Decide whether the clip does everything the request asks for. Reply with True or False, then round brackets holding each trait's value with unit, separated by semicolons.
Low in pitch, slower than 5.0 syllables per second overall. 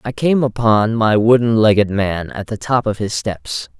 True (110 Hz; 4.4 syllables/s)